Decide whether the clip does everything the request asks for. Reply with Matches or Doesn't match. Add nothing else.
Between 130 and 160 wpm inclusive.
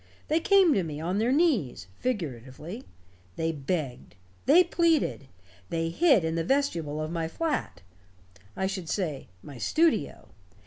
Matches